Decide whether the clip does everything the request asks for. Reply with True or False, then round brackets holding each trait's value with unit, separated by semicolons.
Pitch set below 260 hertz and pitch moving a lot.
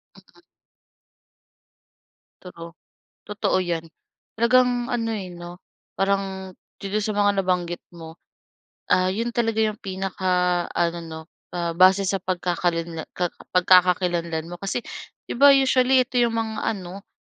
False (185 Hz; 3.7 semitones)